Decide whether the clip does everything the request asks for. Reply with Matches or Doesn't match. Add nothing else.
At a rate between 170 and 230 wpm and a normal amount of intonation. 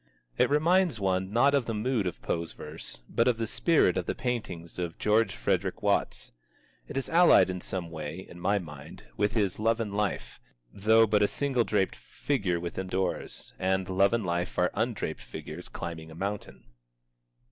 Matches